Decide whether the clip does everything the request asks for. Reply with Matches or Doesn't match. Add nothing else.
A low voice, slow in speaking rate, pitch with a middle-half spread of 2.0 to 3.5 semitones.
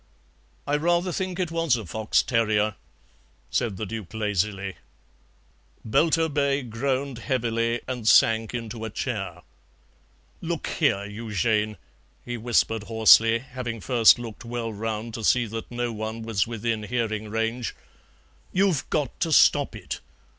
Matches